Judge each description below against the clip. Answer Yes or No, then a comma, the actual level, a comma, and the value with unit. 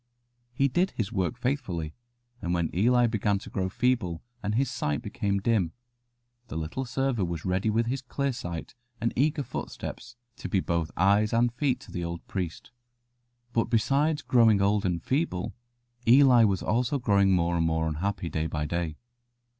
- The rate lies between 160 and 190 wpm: Yes, average, 170 wpm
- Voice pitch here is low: Yes, low, 105 Hz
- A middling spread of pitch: No, wide, 6.1 semitones